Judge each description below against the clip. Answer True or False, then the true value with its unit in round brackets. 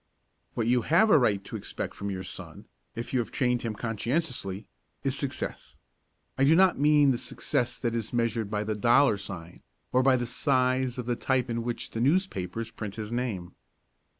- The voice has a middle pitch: False (120 Hz)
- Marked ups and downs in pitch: False (3.2 semitones)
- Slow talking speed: False (190 wpm)